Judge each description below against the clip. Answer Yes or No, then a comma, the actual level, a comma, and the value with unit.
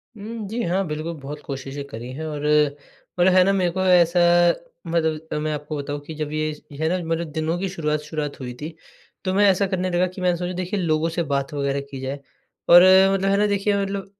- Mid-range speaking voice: Yes, medium, 165 Hz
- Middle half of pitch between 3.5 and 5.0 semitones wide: Yes, average, 3.8 semitones